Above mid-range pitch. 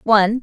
Yes: high, 220 Hz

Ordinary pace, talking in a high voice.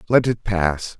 No: average, 180 wpm; low, 100 Hz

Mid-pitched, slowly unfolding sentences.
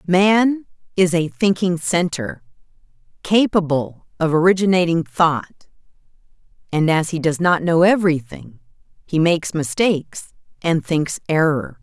Yes: medium, 170 Hz; slow, 110 wpm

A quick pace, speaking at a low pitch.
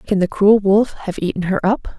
No: fast, 240 wpm; high, 200 Hz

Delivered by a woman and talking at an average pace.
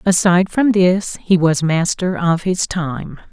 Yes: female; average, 165 wpm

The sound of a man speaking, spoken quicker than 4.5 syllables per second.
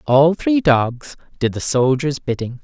No: male; 3.9 syllables/s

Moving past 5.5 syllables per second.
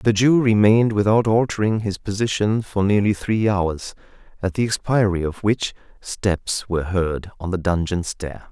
No: 4.6 syllables/s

